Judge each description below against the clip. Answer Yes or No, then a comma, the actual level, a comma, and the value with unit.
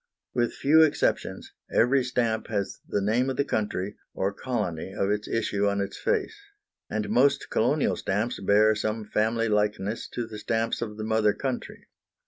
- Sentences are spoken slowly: No, average, 165 wpm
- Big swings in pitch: No, average, 2.9 semitones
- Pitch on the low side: Yes, low, 110 Hz